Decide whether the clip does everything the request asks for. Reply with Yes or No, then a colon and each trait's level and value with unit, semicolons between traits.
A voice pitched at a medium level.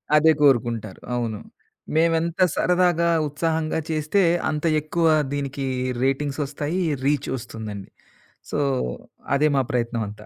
Yes: medium, 145 Hz